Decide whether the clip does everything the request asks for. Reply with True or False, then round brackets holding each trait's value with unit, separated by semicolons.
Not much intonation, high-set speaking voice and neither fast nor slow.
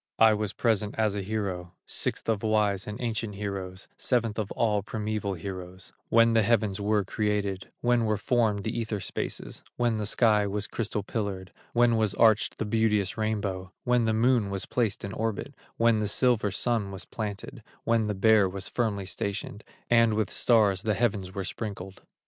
False (2.2 semitones; 105 Hz; 180 wpm)